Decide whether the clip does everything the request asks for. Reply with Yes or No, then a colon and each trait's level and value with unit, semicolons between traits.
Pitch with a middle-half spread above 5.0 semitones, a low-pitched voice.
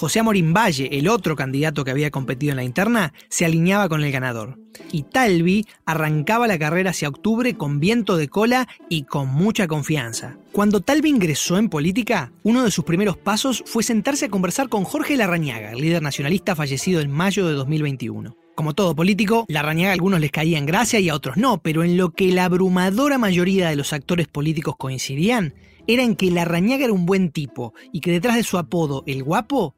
No: wide, 5.6 semitones; medium, 175 Hz